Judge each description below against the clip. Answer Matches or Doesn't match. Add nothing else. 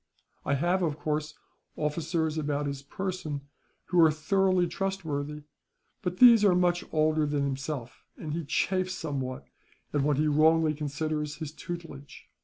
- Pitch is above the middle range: Doesn't match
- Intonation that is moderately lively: Matches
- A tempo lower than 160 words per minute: Matches